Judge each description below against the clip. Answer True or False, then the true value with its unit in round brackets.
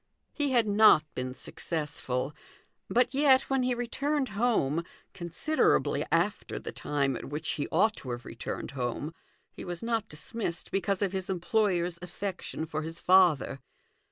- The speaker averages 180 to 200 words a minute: False (150 wpm)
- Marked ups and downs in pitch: True (7.0 semitones)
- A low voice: False (180 Hz)